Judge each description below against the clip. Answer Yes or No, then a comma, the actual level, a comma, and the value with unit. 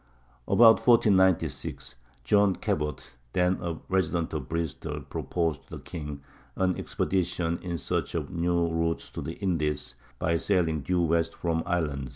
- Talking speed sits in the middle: Yes, average, 150 wpm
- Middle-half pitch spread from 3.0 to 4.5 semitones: No, narrow, 2.4 semitones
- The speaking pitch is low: Yes, very low, 85 Hz